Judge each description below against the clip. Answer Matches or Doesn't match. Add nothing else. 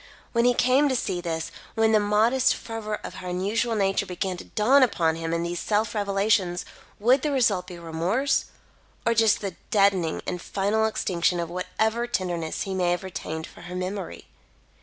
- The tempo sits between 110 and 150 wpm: Doesn't match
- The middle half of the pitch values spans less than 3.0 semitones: Doesn't match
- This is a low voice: Doesn't match